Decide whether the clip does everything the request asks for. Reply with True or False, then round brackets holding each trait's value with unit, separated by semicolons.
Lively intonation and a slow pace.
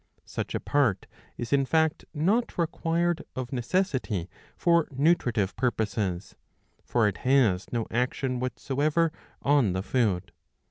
True (6.1 semitones; 130 wpm)